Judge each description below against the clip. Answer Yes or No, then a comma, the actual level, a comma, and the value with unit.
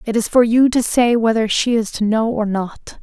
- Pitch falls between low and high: No, high, 225 Hz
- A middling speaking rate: No, fast, 260 wpm